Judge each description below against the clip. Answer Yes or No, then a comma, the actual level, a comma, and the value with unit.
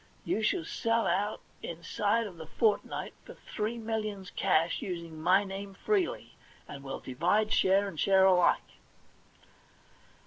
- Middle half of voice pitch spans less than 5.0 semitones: Yes, average, 3.9 semitones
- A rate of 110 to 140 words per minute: Yes, slow, 135 wpm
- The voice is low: No, high, 195 Hz